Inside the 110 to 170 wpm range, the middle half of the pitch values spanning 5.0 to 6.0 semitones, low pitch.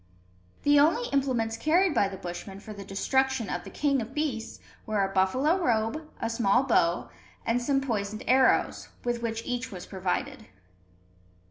No: average, 160 wpm; average, 5.3 semitones; high, 235 Hz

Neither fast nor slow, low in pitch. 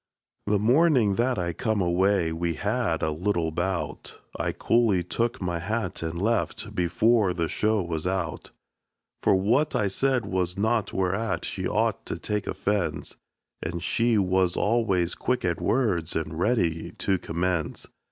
Yes: average, 150 wpm; very low, 95 Hz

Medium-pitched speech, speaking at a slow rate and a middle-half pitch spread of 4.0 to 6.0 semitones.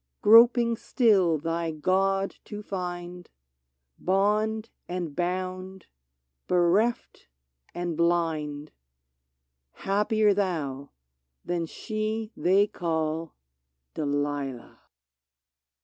Yes: medium, 180 Hz; slow, 80 wpm; average, 4.4 semitones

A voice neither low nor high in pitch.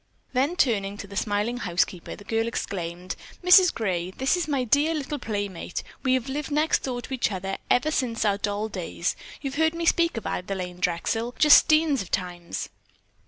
No: high, 225 Hz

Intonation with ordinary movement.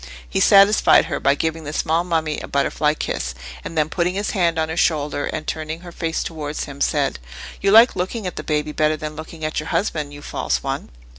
No: narrow, 2.3 semitones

